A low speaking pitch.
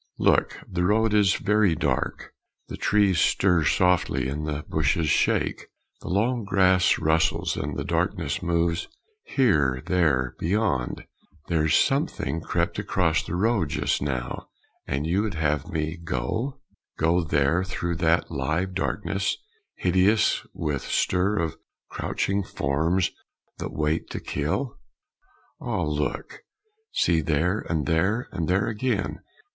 Yes: very low, 85 Hz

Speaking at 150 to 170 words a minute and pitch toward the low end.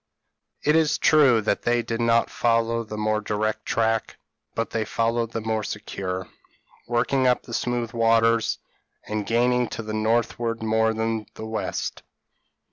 Yes: average, 155 wpm; low, 115 Hz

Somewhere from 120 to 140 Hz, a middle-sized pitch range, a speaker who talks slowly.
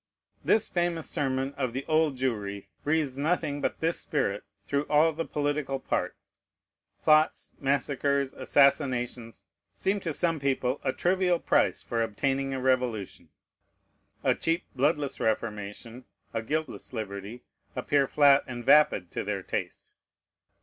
Yes: low, 135 Hz; average, 3.9 semitones; slow, 130 wpm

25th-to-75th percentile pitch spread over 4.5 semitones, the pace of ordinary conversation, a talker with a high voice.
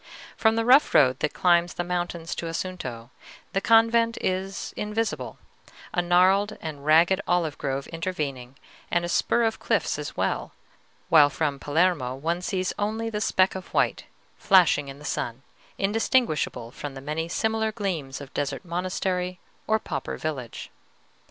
No: average, 5.2 semitones; average, 150 wpm; medium, 175 Hz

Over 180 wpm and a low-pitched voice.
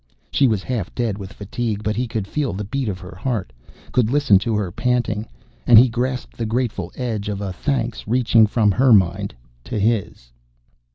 Yes: average, 190 wpm; low, 110 Hz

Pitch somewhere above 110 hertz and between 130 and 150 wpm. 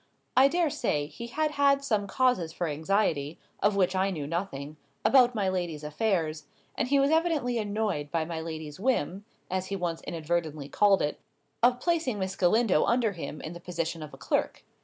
No: high, 190 Hz; average, 185 wpm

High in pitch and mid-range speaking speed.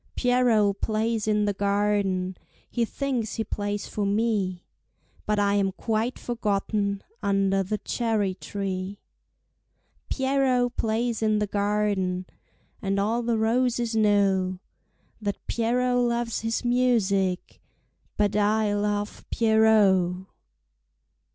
No: high, 210 Hz; slow, 110 wpm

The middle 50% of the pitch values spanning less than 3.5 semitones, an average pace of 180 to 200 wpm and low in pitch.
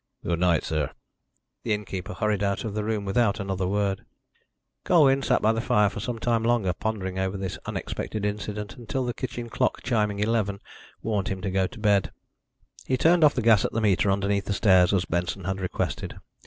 Yes: average, 2.7 semitones; average, 195 wpm; low, 105 Hz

